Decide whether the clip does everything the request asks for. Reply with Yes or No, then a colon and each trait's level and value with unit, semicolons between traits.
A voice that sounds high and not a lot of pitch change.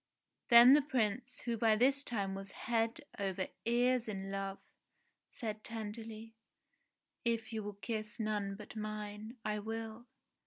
Yes: high, 220 Hz; narrow, 2.2 semitones